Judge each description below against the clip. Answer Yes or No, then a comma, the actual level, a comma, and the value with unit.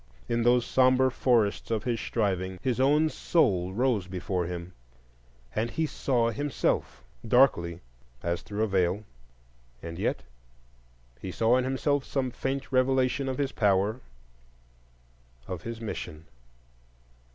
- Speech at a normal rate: No, slow, 125 wpm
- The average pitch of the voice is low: Yes, low, 115 Hz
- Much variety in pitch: Yes, wide, 5.7 semitones